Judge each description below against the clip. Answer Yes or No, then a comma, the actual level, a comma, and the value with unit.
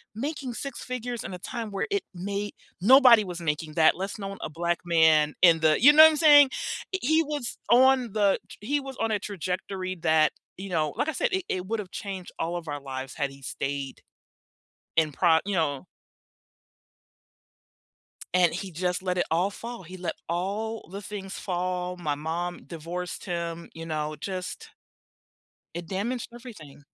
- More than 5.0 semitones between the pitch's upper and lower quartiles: Yes, wide, 5.4 semitones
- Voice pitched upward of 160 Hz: Yes, medium, 185 Hz